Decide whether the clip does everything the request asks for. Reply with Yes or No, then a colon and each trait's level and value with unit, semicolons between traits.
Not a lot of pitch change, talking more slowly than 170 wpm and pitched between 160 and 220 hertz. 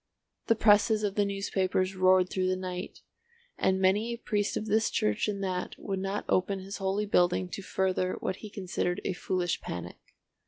No: narrow, 1.7 semitones; average, 185 wpm; high, 190 Hz